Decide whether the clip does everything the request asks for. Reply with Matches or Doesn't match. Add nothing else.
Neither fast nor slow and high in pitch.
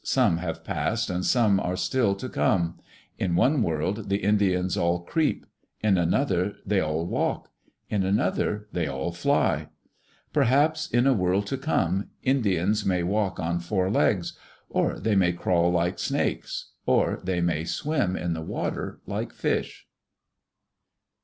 Doesn't match